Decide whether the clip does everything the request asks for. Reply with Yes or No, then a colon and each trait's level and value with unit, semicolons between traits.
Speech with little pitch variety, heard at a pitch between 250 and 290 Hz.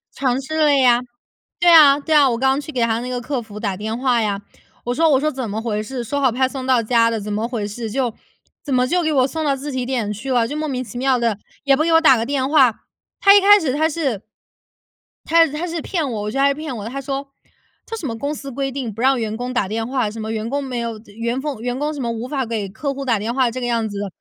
No: average, 3.6 semitones; very high, 255 Hz